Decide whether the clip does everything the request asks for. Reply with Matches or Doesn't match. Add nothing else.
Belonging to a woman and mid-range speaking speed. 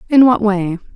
Matches